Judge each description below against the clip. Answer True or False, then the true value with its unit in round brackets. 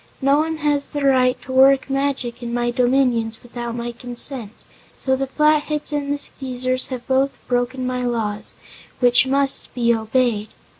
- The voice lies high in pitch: True (255 Hz)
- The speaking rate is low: False (160 wpm)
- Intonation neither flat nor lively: False (2.3 semitones)